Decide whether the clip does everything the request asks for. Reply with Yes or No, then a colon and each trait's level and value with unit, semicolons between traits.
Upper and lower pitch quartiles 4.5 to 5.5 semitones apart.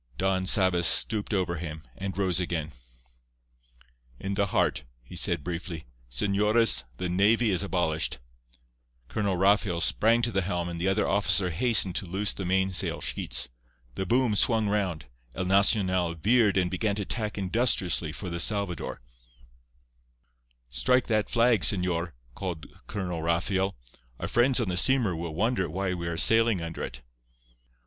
No: average, 3.4 semitones